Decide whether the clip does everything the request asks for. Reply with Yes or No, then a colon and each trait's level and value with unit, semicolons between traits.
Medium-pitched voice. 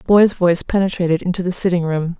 Yes: medium, 180 Hz